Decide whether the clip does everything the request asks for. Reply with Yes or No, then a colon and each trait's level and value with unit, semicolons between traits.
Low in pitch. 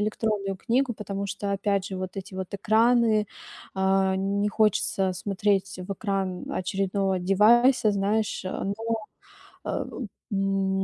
No: high, 195 Hz